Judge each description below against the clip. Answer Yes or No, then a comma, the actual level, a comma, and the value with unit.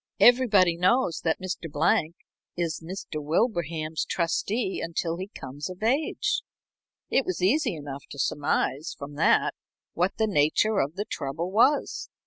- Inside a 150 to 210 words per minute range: No, average, 140 wpm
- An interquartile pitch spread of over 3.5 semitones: Yes, average, 5.0 semitones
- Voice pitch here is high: No, medium, 170 Hz